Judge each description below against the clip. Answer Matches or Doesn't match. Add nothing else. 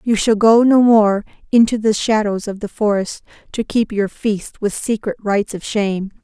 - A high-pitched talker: Matches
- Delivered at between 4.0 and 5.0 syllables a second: Matches